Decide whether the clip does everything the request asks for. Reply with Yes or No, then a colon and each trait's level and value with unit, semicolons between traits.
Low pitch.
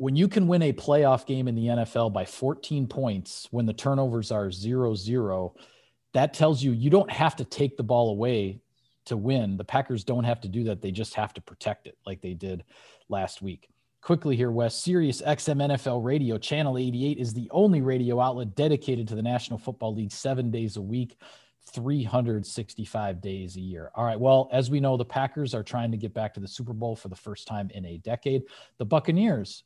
Yes: low, 120 Hz